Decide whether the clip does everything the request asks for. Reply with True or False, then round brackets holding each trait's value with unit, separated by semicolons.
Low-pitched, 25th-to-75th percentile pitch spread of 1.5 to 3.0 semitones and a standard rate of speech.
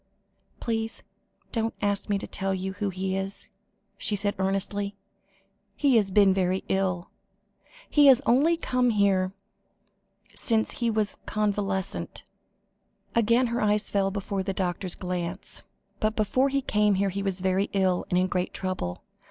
False (200 Hz; 2.5 semitones; 150 wpm)